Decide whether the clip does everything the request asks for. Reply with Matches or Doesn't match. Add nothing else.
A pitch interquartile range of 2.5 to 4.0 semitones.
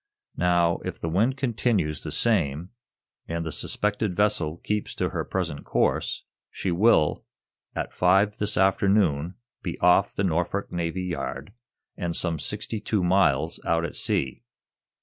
Matches